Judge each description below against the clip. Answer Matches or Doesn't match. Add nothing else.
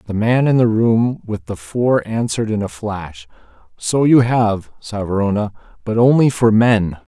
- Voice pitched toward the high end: Doesn't match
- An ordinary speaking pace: Matches